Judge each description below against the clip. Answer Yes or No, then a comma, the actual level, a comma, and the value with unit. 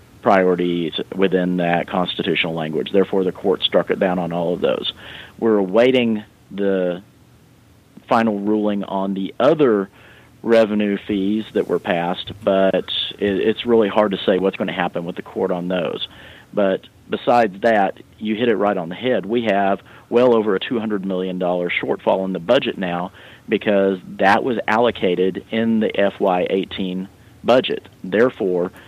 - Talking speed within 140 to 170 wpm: Yes, average, 155 wpm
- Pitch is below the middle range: Yes, low, 100 Hz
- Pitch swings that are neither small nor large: Yes, average, 3.3 semitones